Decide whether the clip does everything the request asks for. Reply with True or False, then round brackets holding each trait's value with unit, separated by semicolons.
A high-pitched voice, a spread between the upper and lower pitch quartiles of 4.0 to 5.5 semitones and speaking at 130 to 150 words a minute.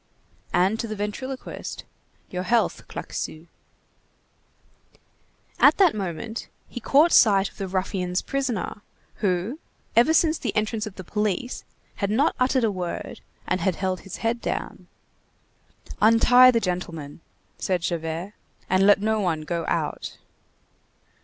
True (205 Hz; 4.3 semitones; 135 wpm)